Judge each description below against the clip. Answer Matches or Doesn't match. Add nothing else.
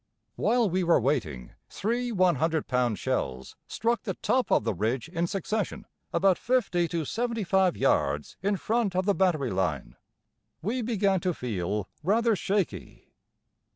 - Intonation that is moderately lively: Doesn't match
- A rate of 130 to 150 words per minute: Matches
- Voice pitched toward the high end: Doesn't match